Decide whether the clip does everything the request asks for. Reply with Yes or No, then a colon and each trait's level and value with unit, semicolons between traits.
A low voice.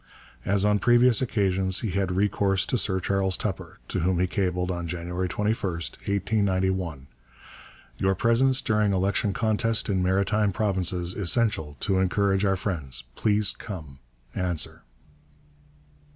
Yes: very low, 95 Hz